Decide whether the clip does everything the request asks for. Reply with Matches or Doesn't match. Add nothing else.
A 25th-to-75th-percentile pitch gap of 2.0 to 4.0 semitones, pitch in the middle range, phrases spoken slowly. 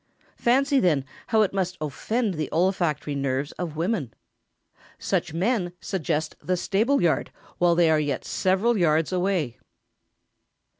Doesn't match